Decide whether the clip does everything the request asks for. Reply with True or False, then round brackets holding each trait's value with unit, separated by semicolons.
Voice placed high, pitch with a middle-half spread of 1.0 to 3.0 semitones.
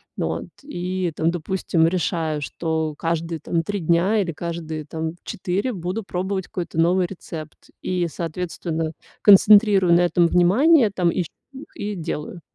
False (175 Hz; 2.4 semitones)